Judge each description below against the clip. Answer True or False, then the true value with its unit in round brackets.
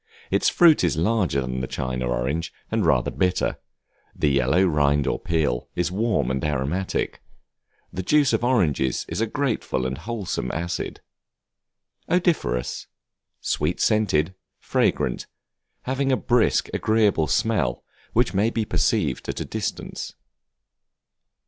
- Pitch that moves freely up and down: True (8.7 semitones)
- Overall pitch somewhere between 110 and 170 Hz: False (90 Hz)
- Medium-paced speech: False (130 wpm)